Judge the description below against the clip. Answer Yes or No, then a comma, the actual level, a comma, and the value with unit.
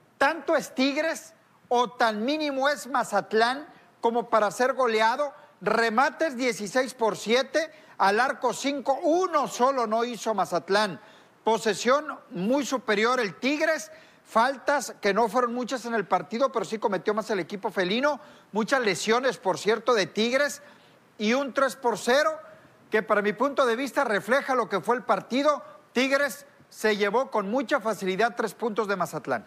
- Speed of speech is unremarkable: Yes, average, 155 wpm